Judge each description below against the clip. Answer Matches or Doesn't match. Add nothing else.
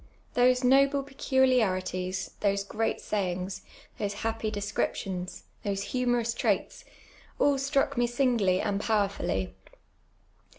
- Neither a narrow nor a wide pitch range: Matches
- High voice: Matches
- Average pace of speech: Doesn't match